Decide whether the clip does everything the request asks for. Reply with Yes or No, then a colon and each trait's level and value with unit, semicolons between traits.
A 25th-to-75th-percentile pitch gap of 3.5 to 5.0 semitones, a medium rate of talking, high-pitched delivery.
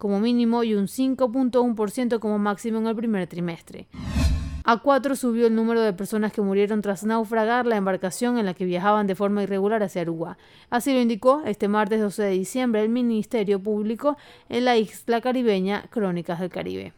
No: average, 3.1 semitones; average, 180 wpm; high, 215 Hz